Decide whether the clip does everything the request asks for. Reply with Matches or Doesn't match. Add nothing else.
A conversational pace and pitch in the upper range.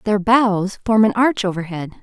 Matches